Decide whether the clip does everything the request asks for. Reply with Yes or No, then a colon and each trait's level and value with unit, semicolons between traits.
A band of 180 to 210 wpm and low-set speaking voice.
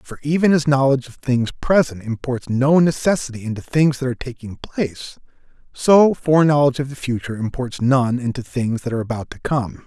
Yes: average, 185 wpm; low, 130 Hz